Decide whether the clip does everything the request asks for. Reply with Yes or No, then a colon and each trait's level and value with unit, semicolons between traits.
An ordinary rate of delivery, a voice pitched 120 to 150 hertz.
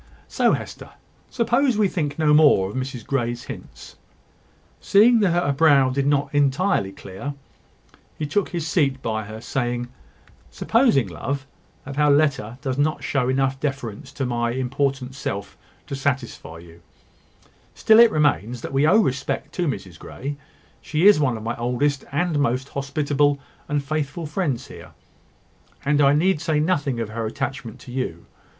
Yes: average, 160 wpm; medium, 140 Hz